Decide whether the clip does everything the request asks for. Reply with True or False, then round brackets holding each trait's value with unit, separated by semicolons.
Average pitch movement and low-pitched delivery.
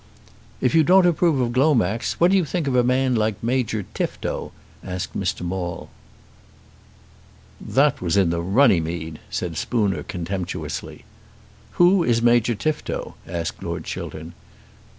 False (7.7 semitones; 115 Hz)